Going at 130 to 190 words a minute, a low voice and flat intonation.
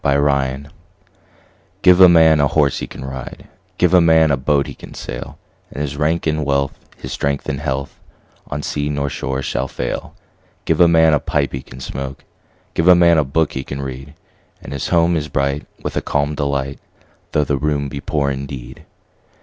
No: average, 200 wpm; very low, 70 Hz; narrow, 2.3 semitones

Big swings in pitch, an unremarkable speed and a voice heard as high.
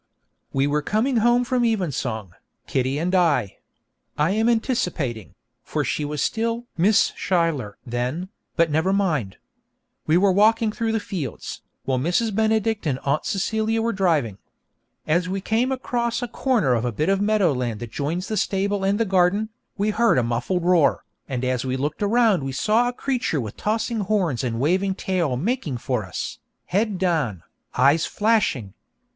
No: wide, 8.3 semitones; average, 170 wpm; medium, 180 Hz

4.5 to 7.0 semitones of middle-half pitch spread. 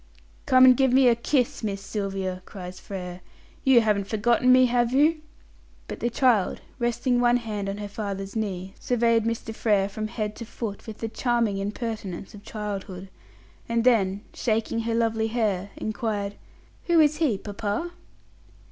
No: average, 3.2 semitones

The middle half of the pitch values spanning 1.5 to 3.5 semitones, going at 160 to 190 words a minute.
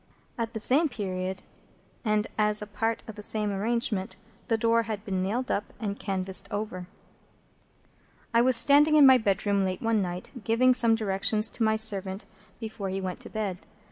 Yes: average, 2.8 semitones; average, 175 wpm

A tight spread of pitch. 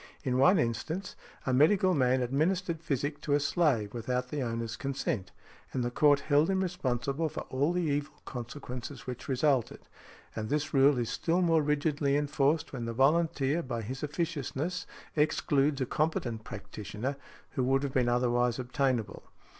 No: average, 3.6 semitones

